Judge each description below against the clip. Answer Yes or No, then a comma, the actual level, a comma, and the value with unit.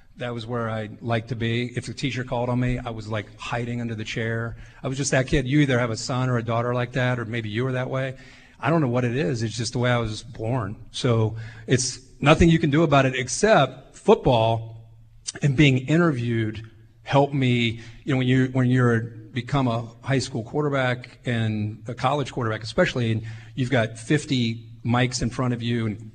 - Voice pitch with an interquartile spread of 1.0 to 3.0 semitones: Yes, narrow, 2.5 semitones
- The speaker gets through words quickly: Yes, fast, 220 wpm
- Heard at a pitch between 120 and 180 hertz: Yes, low, 125 Hz